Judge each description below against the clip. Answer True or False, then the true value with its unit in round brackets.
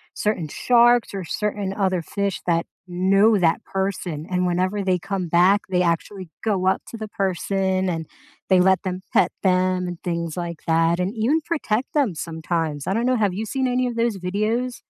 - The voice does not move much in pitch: False (3.2 semitones)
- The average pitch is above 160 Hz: True (190 Hz)